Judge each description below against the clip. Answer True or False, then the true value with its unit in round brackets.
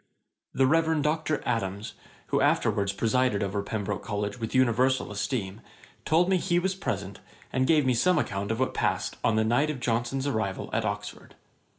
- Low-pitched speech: True (120 Hz)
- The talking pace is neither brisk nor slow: True (180 wpm)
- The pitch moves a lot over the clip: True (5.7 semitones)